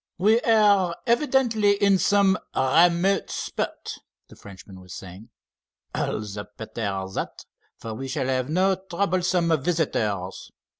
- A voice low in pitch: No, medium, 170 Hz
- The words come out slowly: Yes, slow, 120 wpm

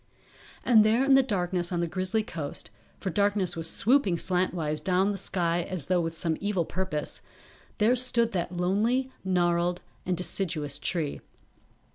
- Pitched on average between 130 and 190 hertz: Yes, medium, 185 Hz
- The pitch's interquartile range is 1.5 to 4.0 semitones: Yes, average, 3.3 semitones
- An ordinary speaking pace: Yes, average, 155 wpm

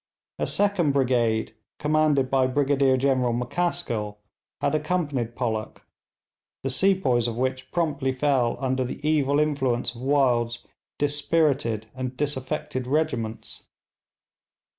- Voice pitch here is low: Yes, low, 130 Hz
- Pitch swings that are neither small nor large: Yes, average, 3.2 semitones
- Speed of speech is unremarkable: No, slow, 110 wpm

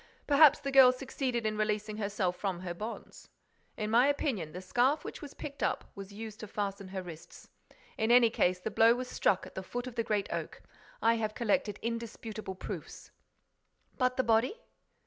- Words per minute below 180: No, average, 185 wpm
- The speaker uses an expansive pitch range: No, average, 3.8 semitones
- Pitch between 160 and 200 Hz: No, high, 220 Hz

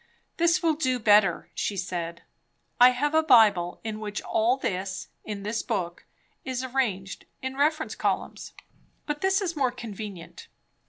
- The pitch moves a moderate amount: No, wide, 6.1 semitones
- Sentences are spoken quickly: No, average, 150 wpm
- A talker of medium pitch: No, high, 230 Hz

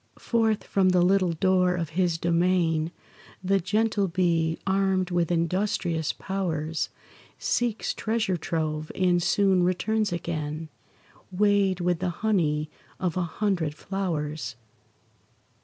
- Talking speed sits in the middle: No, slow, 115 wpm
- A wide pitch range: No, average, 2.9 semitones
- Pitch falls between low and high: Yes, medium, 180 Hz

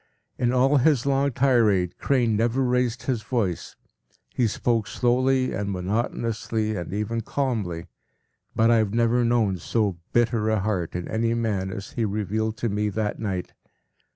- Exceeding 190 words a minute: No, average, 155 wpm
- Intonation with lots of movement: No, average, 2.9 semitones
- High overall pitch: No, low, 115 Hz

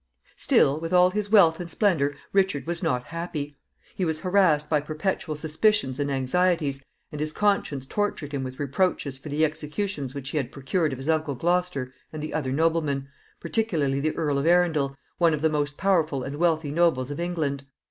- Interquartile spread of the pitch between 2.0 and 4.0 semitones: Yes, average, 3.7 semitones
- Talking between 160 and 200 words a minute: Yes, average, 190 wpm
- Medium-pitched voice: Yes, medium, 155 Hz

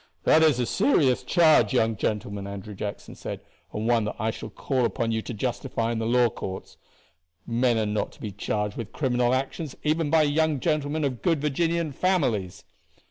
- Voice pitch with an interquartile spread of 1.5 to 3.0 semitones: No, wide, 5.6 semitones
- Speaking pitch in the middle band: No, low, 125 Hz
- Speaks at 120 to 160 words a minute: No, average, 190 wpm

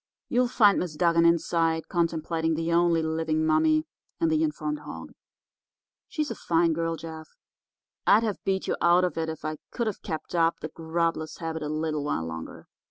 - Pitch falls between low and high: Yes, medium, 165 Hz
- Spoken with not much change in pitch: Yes, narrow, 2.1 semitones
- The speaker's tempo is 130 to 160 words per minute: No, average, 170 wpm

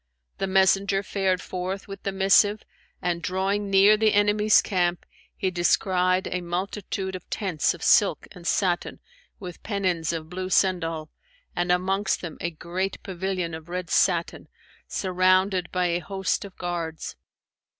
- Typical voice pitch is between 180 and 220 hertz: Yes, medium, 185 Hz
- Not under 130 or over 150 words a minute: Yes, average, 145 wpm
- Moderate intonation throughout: No, narrow, 1.9 semitones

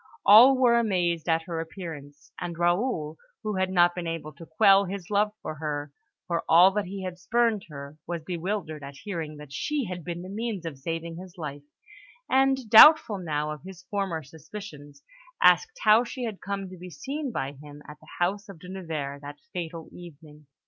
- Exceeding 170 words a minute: Yes, average, 190 wpm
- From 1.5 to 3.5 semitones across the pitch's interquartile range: No, average, 4.5 semitones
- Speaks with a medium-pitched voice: Yes, medium, 175 Hz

